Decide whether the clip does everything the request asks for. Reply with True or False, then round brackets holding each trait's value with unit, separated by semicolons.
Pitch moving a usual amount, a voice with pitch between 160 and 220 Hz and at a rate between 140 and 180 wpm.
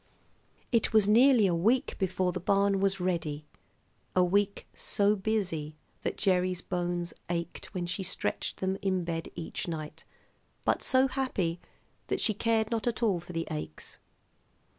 True (3.5 semitones; 185 Hz; 155 wpm)